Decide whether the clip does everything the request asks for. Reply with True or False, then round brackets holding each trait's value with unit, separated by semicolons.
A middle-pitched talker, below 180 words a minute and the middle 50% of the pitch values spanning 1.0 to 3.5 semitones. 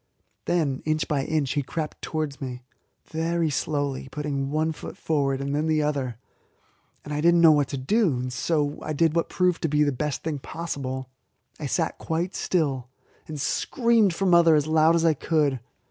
False (150 Hz; 185 wpm; 2.8 semitones)